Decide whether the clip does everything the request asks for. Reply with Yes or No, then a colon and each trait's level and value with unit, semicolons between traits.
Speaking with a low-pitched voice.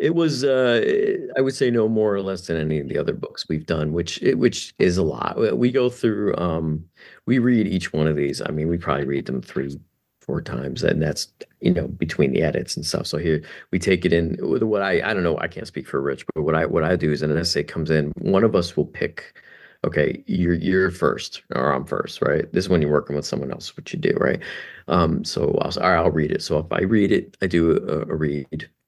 Yes: very low, 85 Hz